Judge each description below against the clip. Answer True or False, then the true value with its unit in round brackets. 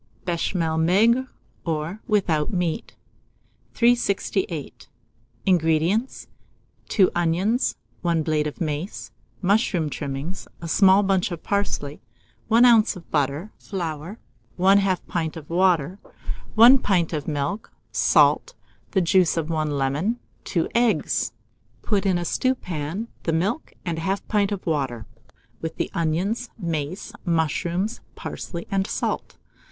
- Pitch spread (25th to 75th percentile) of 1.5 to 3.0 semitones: False (4.1 semitones)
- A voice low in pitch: False (175 Hz)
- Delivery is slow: True (125 wpm)